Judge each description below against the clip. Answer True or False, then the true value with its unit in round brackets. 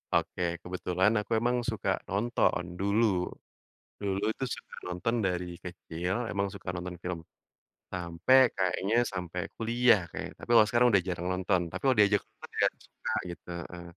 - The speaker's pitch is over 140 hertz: False (95 Hz)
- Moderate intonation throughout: True (3.2 semitones)